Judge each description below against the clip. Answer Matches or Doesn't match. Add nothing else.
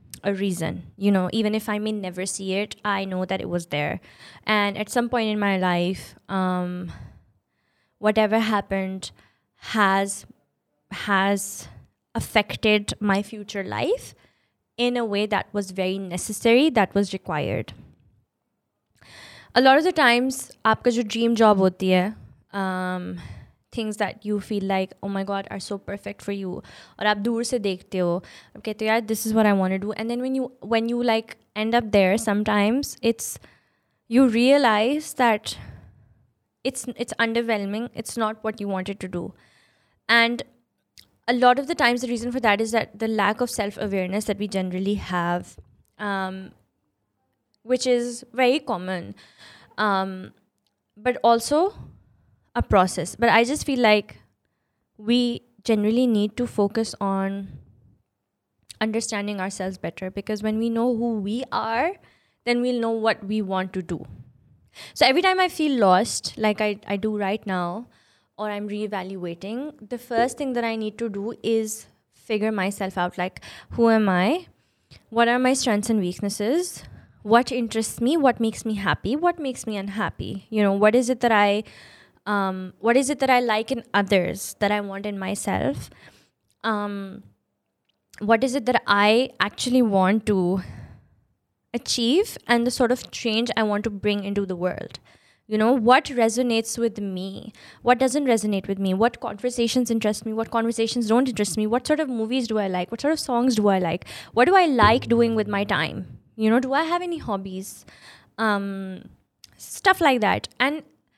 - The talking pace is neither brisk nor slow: Matches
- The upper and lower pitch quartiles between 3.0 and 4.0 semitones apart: Matches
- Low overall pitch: Doesn't match